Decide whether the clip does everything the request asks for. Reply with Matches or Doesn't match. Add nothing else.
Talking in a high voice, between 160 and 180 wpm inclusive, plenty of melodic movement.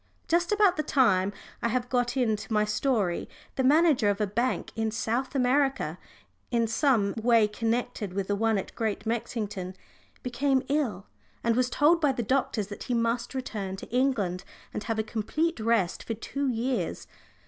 Doesn't match